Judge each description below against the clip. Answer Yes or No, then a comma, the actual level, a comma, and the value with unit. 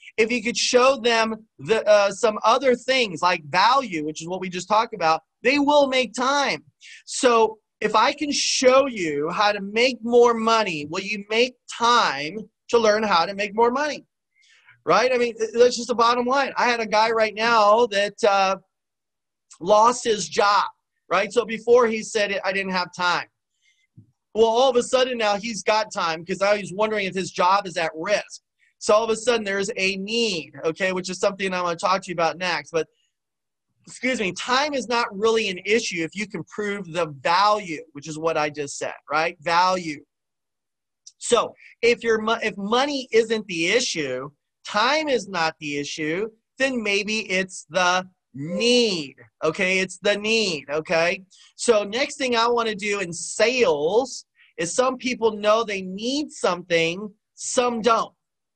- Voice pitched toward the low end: No, high, 215 Hz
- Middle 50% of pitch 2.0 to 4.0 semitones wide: No, average, 4.8 semitones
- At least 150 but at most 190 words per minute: Yes, average, 180 wpm